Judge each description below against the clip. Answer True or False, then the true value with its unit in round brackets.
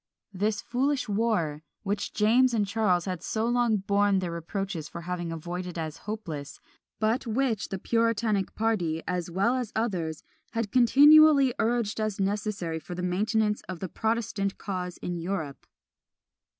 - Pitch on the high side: True (205 Hz)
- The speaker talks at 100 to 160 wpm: True (150 wpm)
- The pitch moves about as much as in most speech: True (4.1 semitones)